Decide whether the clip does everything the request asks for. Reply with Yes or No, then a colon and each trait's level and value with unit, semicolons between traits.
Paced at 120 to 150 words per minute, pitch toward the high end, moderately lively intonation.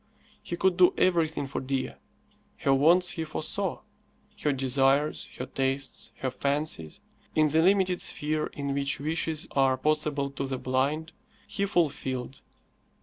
No: average, 140 wpm; medium, 145 Hz; average, 3.0 semitones